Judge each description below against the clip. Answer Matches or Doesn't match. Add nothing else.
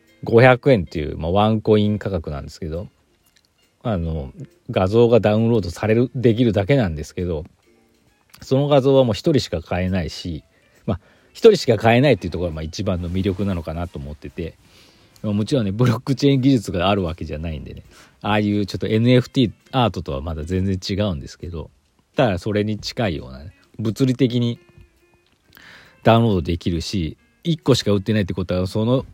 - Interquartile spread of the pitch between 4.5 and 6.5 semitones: Matches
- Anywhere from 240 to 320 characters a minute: Doesn't match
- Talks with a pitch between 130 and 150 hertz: Doesn't match